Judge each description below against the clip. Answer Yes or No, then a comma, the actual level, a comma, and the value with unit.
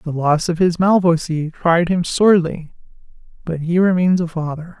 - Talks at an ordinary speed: Yes, average, 150 wpm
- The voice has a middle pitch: Yes, medium, 170 Hz